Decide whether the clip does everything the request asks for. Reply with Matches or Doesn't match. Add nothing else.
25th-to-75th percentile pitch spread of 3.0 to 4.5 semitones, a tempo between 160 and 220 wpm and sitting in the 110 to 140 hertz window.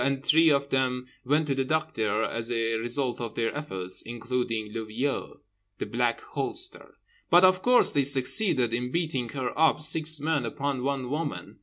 Matches